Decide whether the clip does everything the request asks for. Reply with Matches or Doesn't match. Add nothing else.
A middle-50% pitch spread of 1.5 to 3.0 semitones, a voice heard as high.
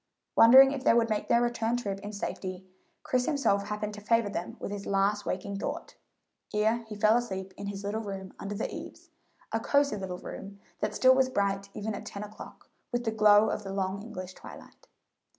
Matches